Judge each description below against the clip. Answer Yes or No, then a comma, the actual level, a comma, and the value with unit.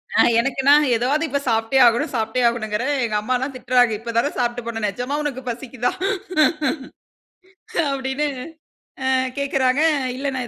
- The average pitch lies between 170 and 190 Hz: No, very high, 250 Hz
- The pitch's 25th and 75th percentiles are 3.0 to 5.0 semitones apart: No, narrow, 2.5 semitones